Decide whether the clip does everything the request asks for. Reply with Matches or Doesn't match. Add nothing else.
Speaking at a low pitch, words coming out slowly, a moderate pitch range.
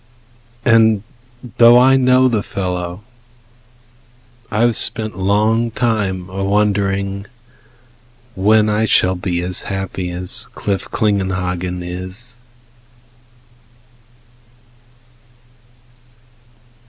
Matches